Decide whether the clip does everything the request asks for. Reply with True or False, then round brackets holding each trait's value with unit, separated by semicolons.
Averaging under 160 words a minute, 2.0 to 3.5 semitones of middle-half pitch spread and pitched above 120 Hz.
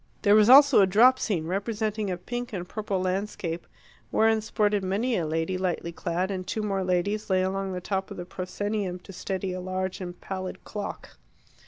False (190 wpm; 2.5 semitones; 190 Hz)